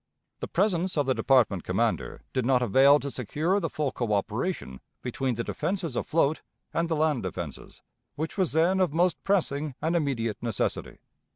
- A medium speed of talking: Yes, average, 165 wpm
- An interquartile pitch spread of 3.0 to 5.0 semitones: No, wide, 5.6 semitones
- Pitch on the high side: No, medium, 140 Hz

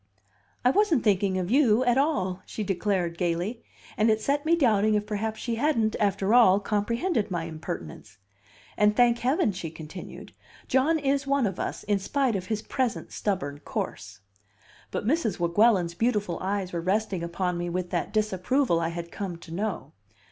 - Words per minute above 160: Yes, average, 170 wpm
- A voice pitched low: No, high, 205 Hz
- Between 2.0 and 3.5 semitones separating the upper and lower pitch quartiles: No, average, 5.0 semitones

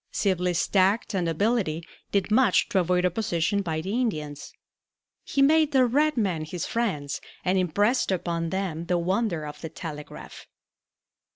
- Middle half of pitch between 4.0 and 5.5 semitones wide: Yes, average, 5.1 semitones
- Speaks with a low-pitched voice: No, medium, 185 Hz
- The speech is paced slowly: No, average, 150 wpm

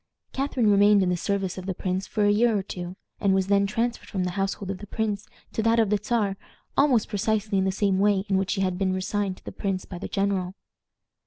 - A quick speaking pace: Yes, fast, 245 wpm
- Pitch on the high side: Yes, high, 200 Hz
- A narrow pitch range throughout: Yes, narrow, 1.8 semitones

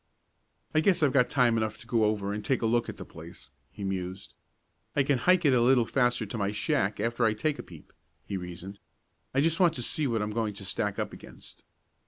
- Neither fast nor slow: No, fast, 235 wpm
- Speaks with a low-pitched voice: Yes, low, 115 Hz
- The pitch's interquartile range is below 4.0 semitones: No, average, 4.6 semitones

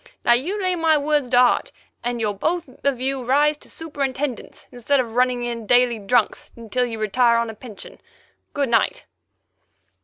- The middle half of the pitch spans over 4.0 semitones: No, average, 3.5 semitones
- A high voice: Yes, very high, 250 Hz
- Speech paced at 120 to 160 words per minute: No, average, 175 wpm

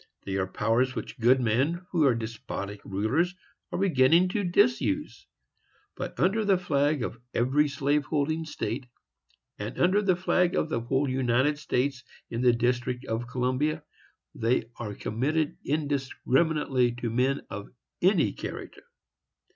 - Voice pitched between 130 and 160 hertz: Yes, low, 135 Hz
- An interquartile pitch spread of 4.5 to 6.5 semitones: Yes, average, 5.0 semitones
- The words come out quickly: No, average, 140 wpm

